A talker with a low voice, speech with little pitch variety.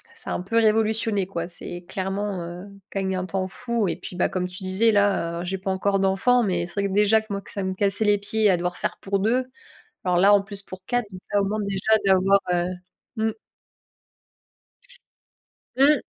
No: high, 195 Hz; narrow, 2.1 semitones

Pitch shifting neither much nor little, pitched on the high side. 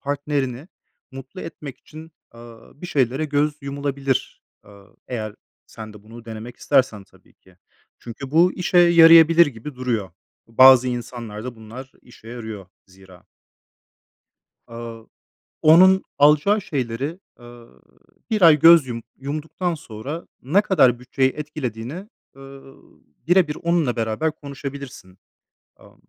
No: average, 5.0 semitones; low, 135 Hz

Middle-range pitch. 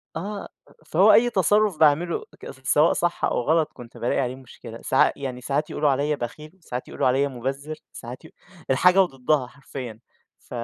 Yes: medium, 145 Hz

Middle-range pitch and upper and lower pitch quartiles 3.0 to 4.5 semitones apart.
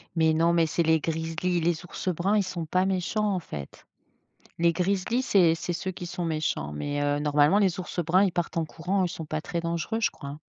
No: medium, 170 Hz; narrow, 2.5 semitones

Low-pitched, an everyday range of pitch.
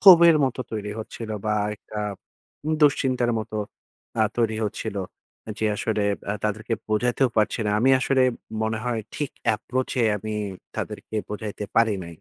Yes: low, 110 Hz; average, 3.1 semitones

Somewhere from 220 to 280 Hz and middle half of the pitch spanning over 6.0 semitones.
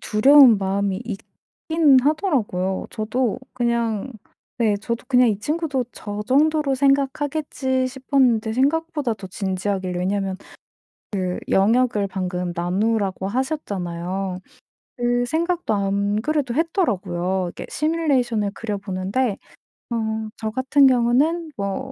No: high, 230 Hz; wide, 5.5 semitones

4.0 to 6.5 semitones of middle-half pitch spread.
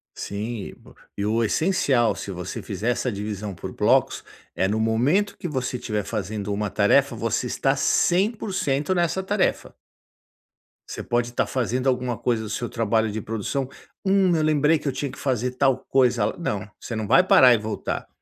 Yes: average, 5.0 semitones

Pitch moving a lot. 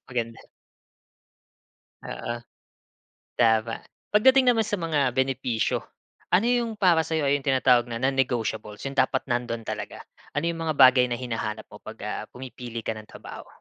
No: average, 4.8 semitones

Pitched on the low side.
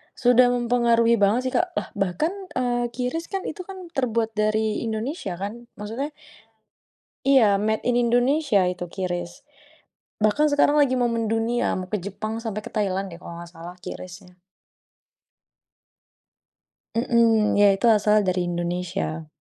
No: high, 220 Hz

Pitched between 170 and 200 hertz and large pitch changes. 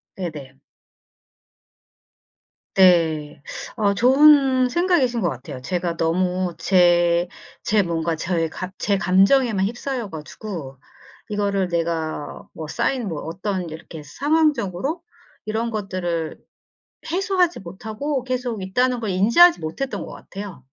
Yes: high, 190 Hz; wide, 6.6 semitones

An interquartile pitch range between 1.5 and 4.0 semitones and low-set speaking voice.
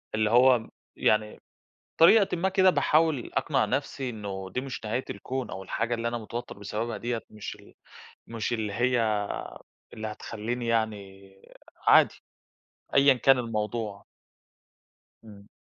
Yes: average, 3.0 semitones; low, 115 Hz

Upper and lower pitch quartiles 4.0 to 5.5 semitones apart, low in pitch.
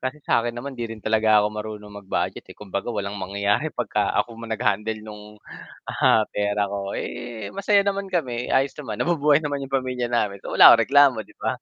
Yes: average, 4.5 semitones; low, 115 Hz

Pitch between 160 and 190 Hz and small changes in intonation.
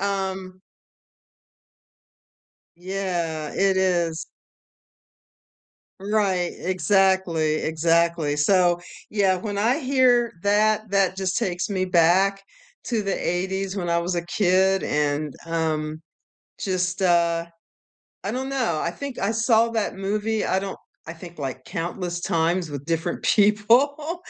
No: medium, 185 Hz; average, 3.2 semitones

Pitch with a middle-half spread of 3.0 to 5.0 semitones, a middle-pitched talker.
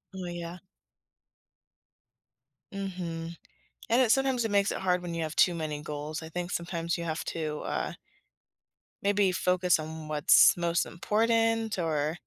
Yes: average, 3.6 semitones; medium, 175 Hz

